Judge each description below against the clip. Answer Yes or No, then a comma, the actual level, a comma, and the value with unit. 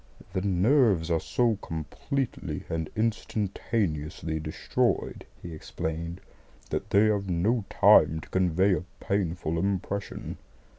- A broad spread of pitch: No, average, 4.1 semitones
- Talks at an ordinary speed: No, slow, 110 wpm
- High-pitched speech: No, very low, 95 Hz